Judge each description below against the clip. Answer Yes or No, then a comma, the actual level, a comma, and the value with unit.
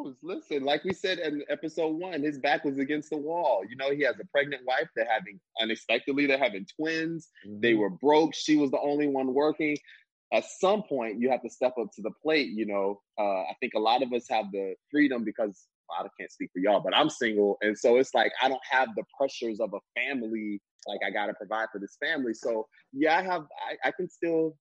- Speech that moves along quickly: Yes, fast, 235 wpm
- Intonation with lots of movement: Yes, wide, 5.7 semitones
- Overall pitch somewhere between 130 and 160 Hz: Yes, medium, 140 Hz